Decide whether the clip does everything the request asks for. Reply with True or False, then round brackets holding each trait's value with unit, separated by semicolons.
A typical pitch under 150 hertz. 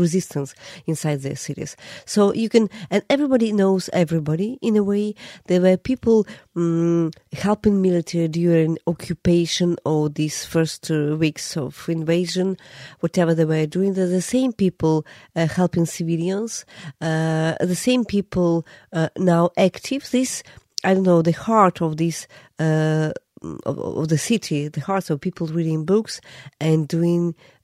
False (170 Hz)